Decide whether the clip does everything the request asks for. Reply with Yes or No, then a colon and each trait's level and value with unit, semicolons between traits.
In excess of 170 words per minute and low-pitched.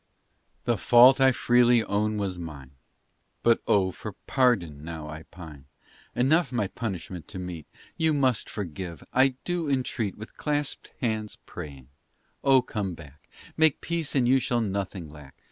No: average, 150 wpm; low, 105 Hz